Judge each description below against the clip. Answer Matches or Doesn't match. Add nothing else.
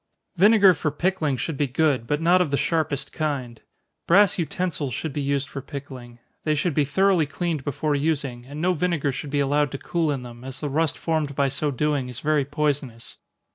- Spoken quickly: Matches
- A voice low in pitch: Doesn't match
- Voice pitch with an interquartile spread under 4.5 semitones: Matches